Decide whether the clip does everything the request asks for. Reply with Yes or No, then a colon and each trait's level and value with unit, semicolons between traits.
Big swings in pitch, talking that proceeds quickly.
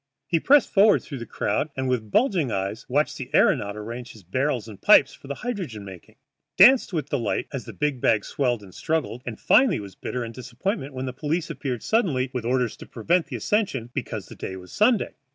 Yes: wide, 6.4 semitones; fast, 210 wpm